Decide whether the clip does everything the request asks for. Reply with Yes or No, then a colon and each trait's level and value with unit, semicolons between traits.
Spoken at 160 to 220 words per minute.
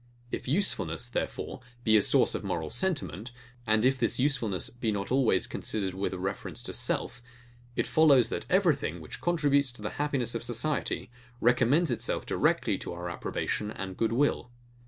Yes: average, 170 wpm